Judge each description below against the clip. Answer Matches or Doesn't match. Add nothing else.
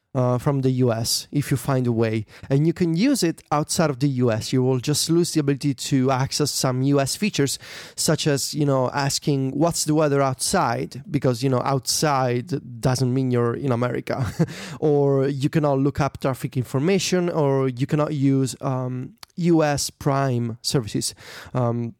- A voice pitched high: Doesn't match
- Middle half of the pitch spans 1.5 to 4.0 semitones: Matches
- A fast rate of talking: Doesn't match